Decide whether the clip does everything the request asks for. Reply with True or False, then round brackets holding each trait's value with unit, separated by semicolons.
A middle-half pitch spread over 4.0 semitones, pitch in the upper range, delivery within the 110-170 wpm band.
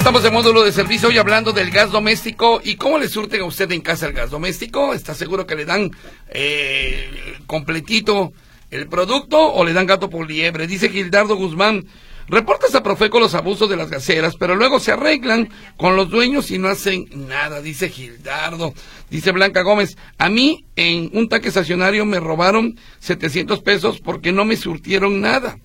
False (4.5 semitones; 195 Hz; 180 wpm)